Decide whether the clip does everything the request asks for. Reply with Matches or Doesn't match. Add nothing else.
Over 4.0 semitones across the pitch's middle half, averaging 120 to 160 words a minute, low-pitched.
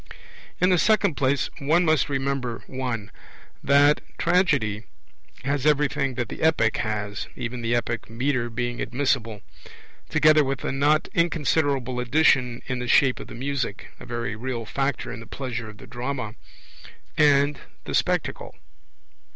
Doesn't match